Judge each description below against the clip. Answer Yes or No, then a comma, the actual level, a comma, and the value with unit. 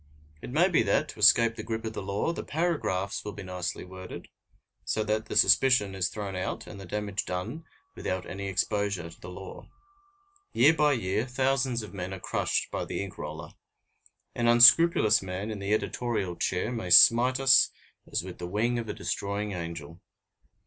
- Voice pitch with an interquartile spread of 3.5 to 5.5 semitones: Yes, average, 4.1 semitones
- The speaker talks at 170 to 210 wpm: Yes, average, 185 wpm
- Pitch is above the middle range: No, low, 105 Hz